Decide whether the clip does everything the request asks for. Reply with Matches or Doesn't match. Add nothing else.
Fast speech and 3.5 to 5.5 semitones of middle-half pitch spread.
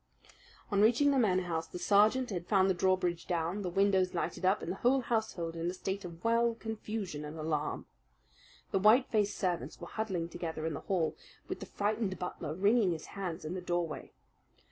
Doesn't match